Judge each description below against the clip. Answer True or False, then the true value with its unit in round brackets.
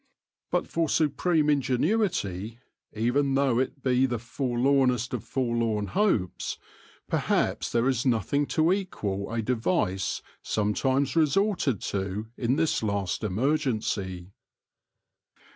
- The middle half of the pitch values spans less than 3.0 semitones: False (5.0 semitones)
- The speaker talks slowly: True (110 wpm)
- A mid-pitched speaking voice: False (125 Hz)